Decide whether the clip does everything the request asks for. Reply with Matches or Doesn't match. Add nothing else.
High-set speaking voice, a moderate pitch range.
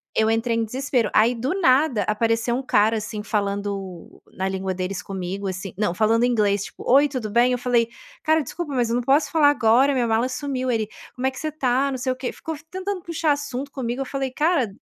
Matches